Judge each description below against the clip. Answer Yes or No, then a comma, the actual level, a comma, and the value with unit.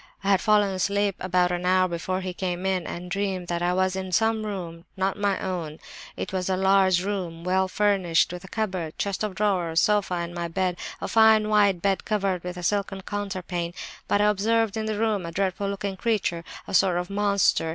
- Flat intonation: Yes, narrow, 2.3 semitones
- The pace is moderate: No, fast, 210 wpm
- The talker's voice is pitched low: No, high, 190 Hz